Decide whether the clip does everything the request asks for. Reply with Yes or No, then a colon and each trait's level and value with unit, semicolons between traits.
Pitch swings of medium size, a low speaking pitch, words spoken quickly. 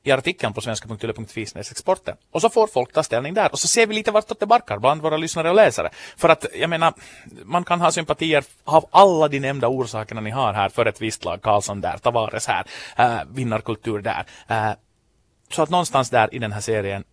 No: wide, 7.1 semitones; low, 130 Hz; fast, 210 wpm